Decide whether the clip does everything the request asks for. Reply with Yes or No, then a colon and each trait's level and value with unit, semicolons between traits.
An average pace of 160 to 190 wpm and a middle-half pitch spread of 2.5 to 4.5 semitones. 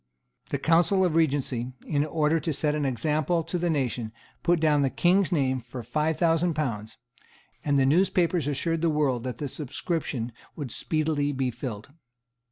Yes: average, 170 wpm; average, 3.8 semitones